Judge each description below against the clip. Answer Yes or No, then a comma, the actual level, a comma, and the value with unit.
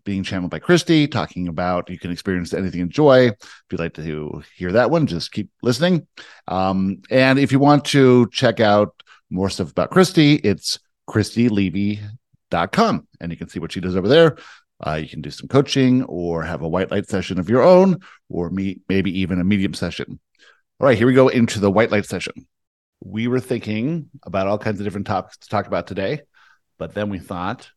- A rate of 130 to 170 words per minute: No, fast, 205 wpm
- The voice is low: Yes, low, 100 Hz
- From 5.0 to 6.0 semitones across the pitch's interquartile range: Yes, wide, 5.6 semitones